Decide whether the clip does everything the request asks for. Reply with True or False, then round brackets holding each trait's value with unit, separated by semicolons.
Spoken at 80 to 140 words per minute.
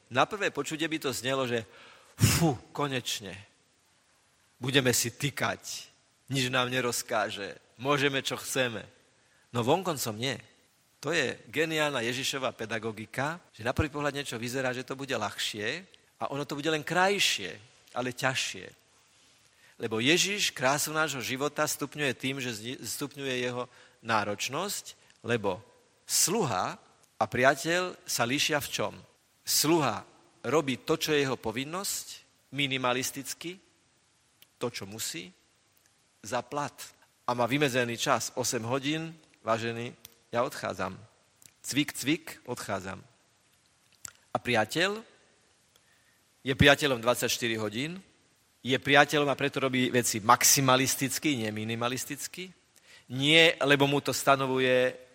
True (120 wpm)